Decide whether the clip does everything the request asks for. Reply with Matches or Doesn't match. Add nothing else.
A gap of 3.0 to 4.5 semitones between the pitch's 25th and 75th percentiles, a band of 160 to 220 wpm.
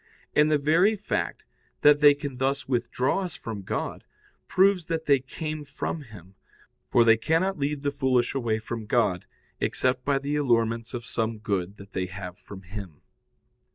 Doesn't match